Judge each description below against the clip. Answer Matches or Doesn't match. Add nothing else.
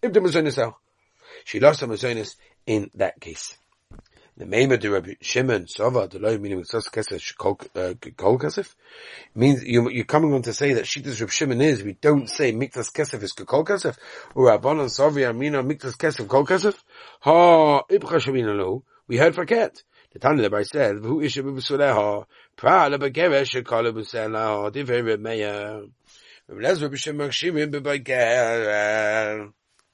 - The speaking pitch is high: Doesn't match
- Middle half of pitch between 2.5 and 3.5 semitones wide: Doesn't match